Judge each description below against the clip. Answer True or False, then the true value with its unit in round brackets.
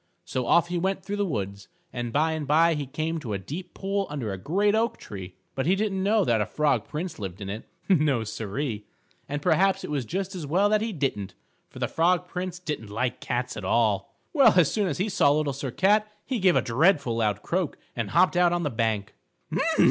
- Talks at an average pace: False (225 wpm)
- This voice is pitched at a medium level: True (150 Hz)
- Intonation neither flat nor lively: False (8.2 semitones)